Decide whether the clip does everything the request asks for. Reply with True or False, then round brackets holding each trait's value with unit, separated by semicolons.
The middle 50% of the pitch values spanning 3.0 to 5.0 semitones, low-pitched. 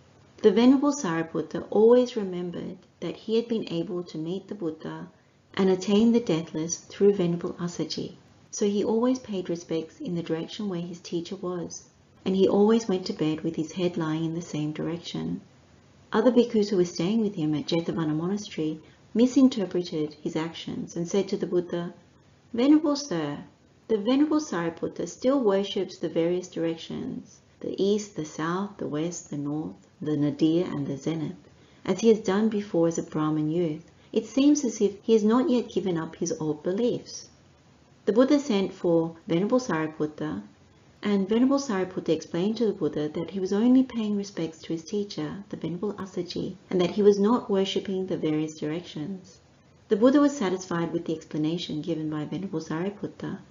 False (4.3 semitones; 180 Hz)